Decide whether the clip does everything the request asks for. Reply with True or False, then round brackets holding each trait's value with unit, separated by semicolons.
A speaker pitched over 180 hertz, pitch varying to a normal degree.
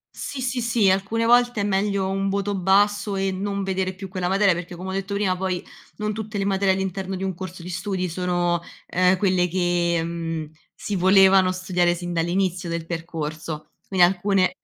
False (190 Hz; 2.0 semitones)